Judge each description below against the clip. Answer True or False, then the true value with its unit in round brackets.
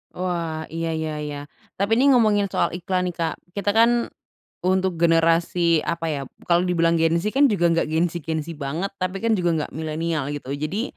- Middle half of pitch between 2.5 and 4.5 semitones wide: True (2.8 semitones)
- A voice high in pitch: False (170 Hz)